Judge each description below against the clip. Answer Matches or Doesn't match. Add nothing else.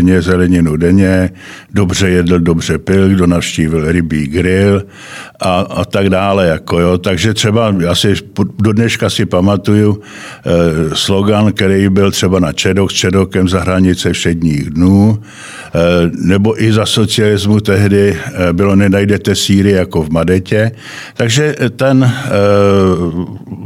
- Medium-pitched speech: Doesn't match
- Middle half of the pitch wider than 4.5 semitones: Doesn't match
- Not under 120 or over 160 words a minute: Matches